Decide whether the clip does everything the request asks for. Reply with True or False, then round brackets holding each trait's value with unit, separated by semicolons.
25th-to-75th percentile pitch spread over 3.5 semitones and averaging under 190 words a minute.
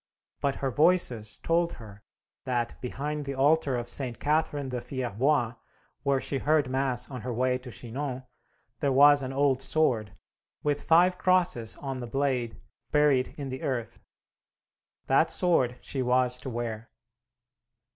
False (2.9 semitones; 145 wpm)